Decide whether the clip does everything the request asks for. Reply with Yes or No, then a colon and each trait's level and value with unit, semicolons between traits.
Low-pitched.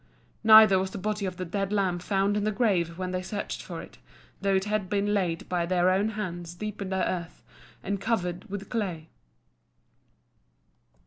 No: high, 195 Hz